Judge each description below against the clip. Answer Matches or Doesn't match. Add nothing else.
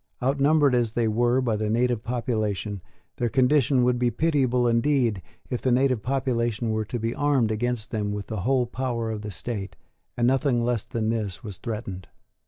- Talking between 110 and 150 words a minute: Doesn't match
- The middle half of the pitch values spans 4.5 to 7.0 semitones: Doesn't match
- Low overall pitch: Matches